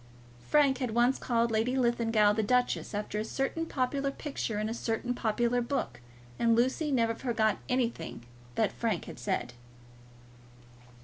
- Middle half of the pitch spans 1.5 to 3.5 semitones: Yes, narrow, 2.6 semitones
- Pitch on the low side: No, high, 235 Hz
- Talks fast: No, average, 145 wpm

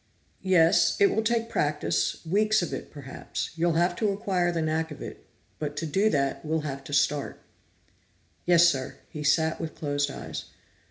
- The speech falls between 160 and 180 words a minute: Yes, average, 175 wpm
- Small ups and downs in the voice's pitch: No, average, 3.6 semitones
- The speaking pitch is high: No, medium, 160 Hz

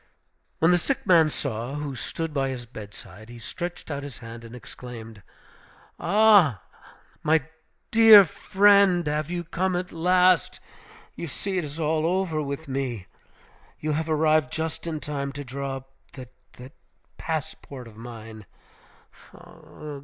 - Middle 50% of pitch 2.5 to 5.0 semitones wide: No, wide, 5.4 semitones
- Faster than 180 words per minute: No, average, 145 wpm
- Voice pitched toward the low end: No, medium, 150 Hz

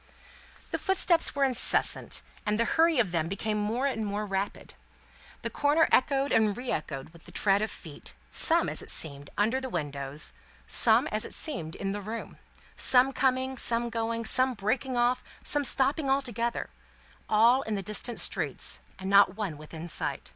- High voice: Yes, high, 225 Hz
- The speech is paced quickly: No, average, 175 wpm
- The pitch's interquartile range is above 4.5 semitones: Yes, average, 5.0 semitones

